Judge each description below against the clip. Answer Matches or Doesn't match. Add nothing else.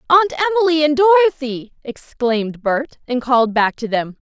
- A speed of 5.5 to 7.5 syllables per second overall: Matches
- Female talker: Matches